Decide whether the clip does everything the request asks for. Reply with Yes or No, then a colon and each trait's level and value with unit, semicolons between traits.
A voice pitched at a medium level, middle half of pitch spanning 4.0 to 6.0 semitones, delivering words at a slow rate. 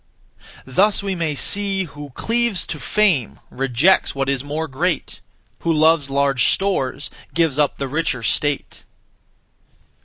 Yes: medium, 150 Hz; average, 5.3 semitones; slow, 130 wpm